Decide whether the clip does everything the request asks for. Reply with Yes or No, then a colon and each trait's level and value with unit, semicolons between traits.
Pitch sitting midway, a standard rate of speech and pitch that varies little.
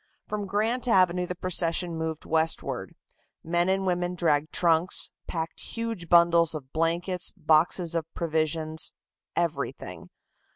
No: medium, 170 Hz; slow, 120 wpm; narrow, 2.1 semitones